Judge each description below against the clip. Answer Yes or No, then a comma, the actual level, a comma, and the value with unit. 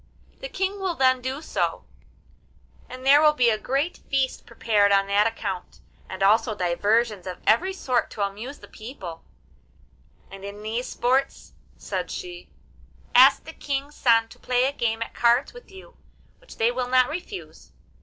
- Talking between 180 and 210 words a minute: No, average, 165 wpm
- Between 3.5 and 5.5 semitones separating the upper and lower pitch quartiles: Yes, average, 4.7 semitones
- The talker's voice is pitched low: No, high, 245 Hz